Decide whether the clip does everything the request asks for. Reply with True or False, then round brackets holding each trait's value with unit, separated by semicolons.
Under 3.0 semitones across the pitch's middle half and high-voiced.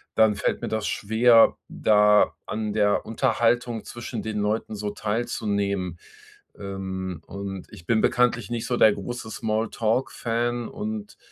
False (2.5 semitones; 110 Hz)